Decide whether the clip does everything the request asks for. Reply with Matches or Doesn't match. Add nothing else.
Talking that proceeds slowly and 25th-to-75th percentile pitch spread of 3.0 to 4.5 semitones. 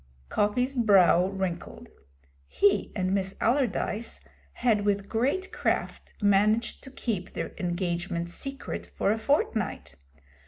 Matches